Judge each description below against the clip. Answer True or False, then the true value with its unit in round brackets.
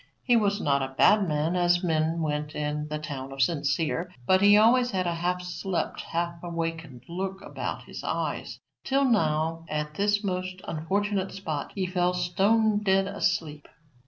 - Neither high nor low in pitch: True (175 Hz)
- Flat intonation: False (4.2 semitones)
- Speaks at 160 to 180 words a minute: True (165 wpm)